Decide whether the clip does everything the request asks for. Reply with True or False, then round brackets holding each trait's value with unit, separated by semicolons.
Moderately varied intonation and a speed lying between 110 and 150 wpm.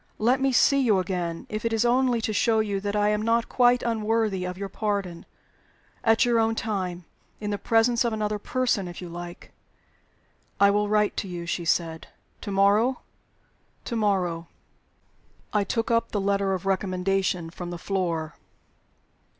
False (3.7 semitones; 165 wpm)